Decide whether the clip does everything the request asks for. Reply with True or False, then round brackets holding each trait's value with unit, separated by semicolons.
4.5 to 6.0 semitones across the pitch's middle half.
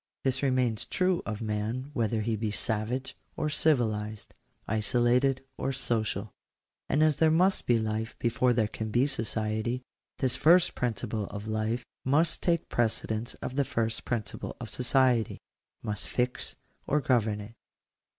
False (3.4 semitones)